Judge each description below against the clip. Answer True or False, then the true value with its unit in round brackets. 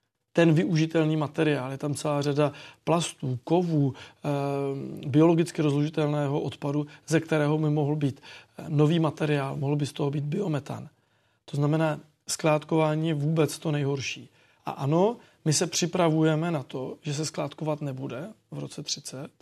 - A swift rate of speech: False (140 wpm)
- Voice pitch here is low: False (150 Hz)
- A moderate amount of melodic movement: False (1.8 semitones)